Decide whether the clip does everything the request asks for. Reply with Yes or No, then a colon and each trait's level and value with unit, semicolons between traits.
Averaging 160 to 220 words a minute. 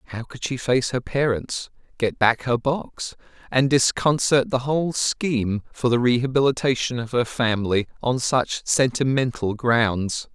No: average, 145 wpm